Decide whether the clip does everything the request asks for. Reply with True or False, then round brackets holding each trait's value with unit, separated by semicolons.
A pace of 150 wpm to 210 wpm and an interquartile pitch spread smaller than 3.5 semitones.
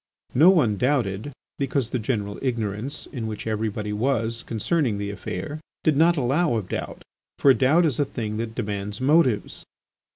False (160 wpm; 5.0 semitones)